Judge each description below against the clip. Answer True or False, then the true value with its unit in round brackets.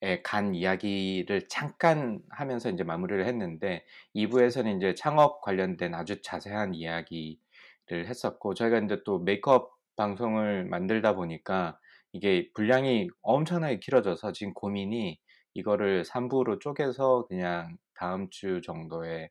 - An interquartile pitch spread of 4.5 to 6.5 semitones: True (5.6 semitones)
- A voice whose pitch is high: False (100 Hz)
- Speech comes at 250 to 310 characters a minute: True (300 characters per minute)